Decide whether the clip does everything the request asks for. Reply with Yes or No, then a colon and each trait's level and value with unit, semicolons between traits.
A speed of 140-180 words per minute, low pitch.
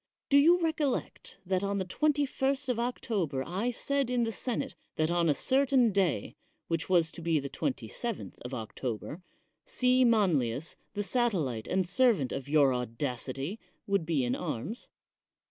No: average, 160 wpm; high, 190 Hz